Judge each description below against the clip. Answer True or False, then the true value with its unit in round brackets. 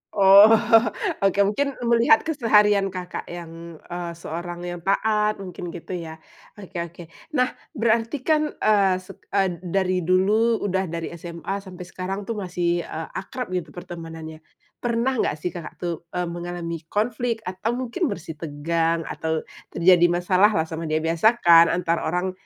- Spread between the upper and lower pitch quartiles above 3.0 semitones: True (3.7 semitones)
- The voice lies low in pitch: False (180 Hz)